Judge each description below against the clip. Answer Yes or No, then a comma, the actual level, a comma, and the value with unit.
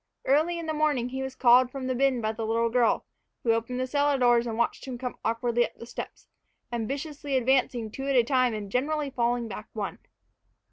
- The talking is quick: Yes, fast, 215 wpm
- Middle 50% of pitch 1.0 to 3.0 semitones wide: Yes, narrow, 2.6 semitones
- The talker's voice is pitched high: Yes, very high, 250 Hz